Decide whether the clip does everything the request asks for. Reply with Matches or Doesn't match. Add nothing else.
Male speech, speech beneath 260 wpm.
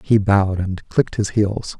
Matches